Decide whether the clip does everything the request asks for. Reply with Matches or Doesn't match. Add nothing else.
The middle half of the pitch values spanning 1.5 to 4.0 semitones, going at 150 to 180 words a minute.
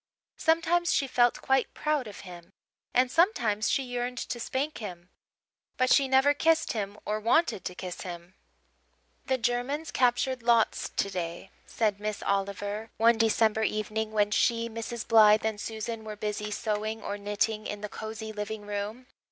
Matches